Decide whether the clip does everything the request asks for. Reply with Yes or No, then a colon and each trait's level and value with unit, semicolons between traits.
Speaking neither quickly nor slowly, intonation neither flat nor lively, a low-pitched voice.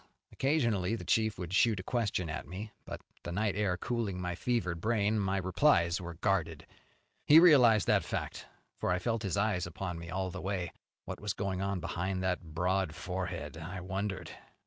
Yes: average, 185 wpm; average, 3.1 semitones; very low, 95 Hz